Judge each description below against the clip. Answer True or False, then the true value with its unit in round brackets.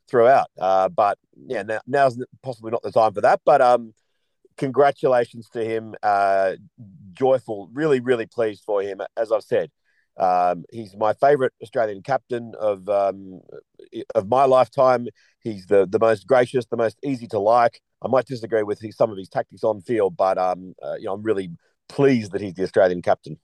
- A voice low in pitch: True (115 Hz)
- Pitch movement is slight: False (4.4 semitones)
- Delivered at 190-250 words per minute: False (180 wpm)